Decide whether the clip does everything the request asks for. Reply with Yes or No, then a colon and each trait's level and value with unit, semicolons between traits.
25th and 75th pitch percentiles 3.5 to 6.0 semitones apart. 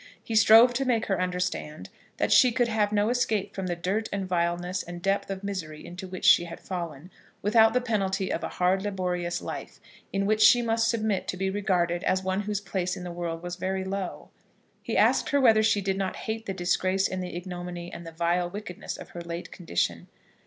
No: average, 3.0 semitones